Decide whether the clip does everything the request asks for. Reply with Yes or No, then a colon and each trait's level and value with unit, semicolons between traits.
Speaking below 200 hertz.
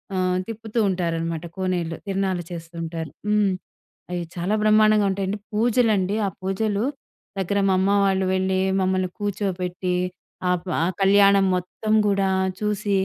Yes: high, 190 Hz